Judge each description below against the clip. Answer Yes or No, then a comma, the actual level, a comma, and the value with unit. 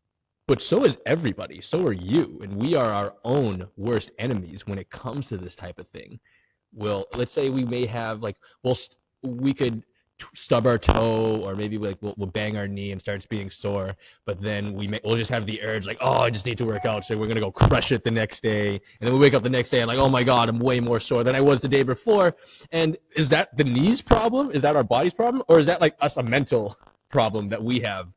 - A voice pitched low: Yes, low, 115 Hz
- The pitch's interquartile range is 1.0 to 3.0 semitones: No, average, 4.0 semitones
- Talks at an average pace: No, fast, 260 wpm